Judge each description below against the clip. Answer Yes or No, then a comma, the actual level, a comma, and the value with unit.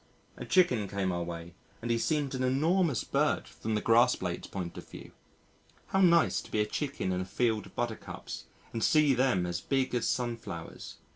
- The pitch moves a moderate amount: No, wide, 5.8 semitones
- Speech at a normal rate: Yes, average, 195 wpm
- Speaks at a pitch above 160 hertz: No, low, 115 Hz